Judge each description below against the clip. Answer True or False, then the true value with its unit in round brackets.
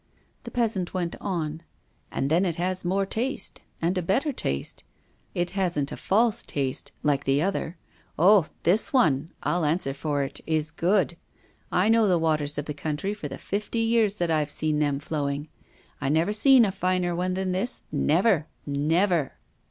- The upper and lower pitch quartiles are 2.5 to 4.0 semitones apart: False (4.6 semitones)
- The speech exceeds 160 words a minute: True (175 wpm)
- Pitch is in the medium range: True (175 Hz)